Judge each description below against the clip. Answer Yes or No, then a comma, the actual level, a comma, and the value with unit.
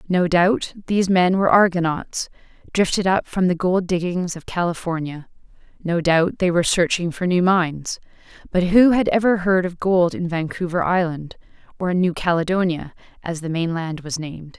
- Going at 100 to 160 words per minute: No, average, 170 wpm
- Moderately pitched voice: Yes, medium, 175 Hz